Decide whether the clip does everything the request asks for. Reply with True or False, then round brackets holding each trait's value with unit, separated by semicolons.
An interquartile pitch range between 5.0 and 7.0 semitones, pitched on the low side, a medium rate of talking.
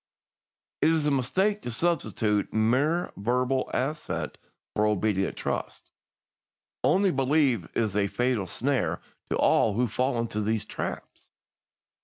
False (5.3 semitones; 125 Hz; 125 wpm)